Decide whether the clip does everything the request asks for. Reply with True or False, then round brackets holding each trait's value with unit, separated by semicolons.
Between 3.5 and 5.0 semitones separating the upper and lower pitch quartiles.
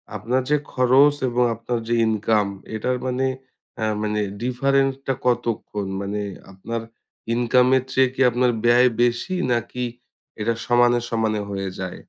False (2.6 semitones)